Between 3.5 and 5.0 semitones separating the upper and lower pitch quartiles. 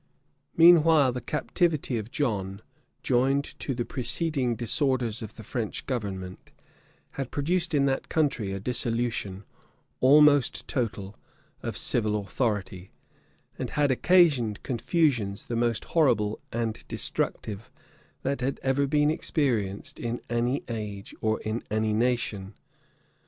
Yes: average, 4.7 semitones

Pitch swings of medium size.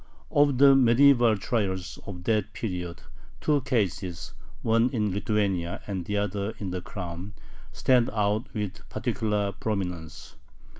Yes: average, 3.8 semitones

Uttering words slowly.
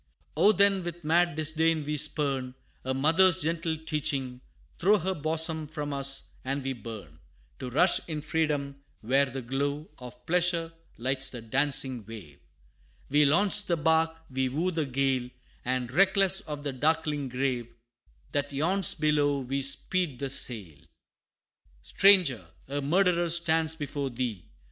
No: average, 145 wpm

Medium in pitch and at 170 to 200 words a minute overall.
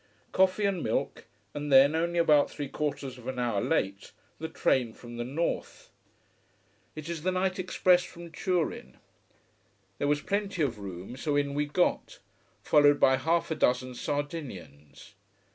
No: medium, 145 Hz; average, 155 wpm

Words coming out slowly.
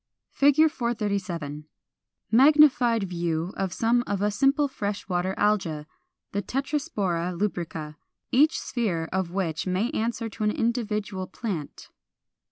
Yes: slow, 125 wpm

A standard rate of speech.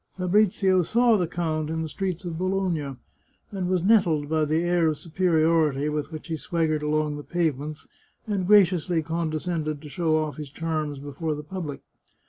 Yes: average, 170 wpm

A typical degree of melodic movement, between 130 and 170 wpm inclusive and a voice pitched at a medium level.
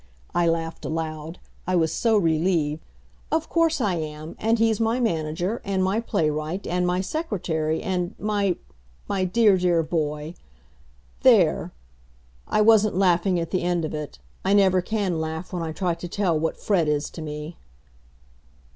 Yes: average, 4.0 semitones; average, 160 wpm; medium, 175 Hz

